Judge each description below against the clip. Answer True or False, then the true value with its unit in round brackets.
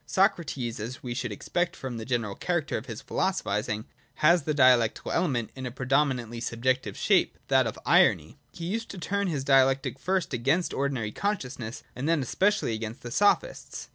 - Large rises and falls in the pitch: True (6.1 semitones)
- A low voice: True (130 Hz)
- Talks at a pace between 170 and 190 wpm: True (175 wpm)